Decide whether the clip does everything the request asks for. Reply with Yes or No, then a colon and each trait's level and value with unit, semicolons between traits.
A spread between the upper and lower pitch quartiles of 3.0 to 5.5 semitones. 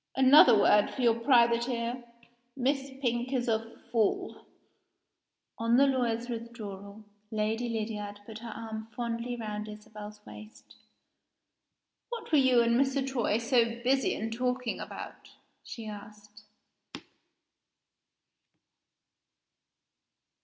No: narrow, 2.5 semitones